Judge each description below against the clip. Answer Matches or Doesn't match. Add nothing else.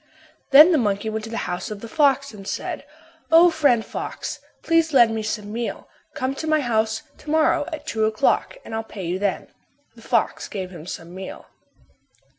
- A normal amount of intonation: Doesn't match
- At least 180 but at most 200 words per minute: Matches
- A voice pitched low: Doesn't match